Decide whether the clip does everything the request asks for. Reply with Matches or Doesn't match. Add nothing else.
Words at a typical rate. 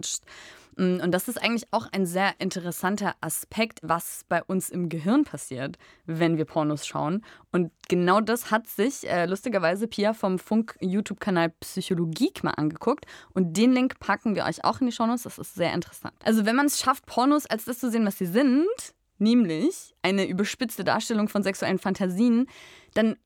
Matches